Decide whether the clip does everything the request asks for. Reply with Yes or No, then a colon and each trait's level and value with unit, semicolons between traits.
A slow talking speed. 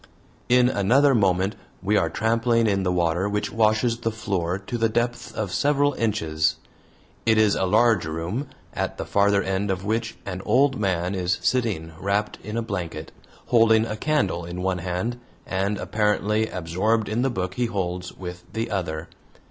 No: average, 170 wpm